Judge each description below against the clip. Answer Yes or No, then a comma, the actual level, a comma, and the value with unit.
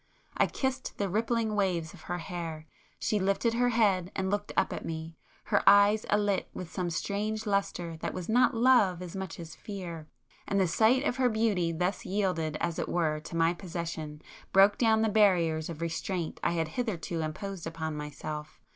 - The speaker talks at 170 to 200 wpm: Yes, average, 180 wpm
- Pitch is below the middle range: No, medium, 185 Hz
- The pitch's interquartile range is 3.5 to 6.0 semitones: Yes, average, 4.1 semitones